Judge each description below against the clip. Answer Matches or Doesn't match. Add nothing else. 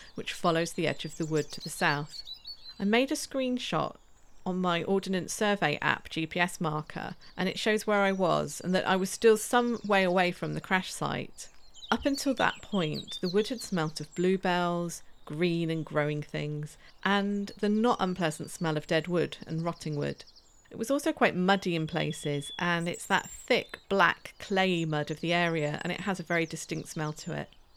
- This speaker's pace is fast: Doesn't match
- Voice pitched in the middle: Matches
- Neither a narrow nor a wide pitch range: Matches